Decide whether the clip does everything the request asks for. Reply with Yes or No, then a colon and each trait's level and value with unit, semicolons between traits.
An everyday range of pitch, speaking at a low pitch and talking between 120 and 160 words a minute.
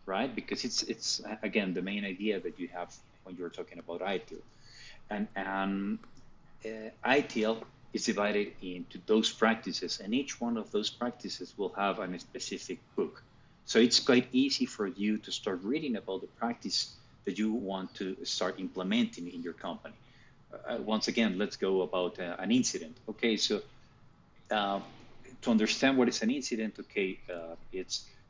No: average, 3.5 semitones; low, 110 Hz; average, 170 wpm